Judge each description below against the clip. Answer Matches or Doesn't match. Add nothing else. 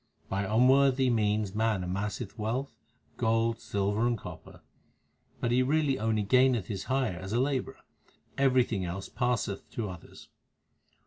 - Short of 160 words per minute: Matches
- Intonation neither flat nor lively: Matches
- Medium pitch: Doesn't match